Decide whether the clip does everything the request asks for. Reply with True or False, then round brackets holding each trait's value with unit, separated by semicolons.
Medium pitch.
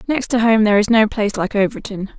False (215 Hz)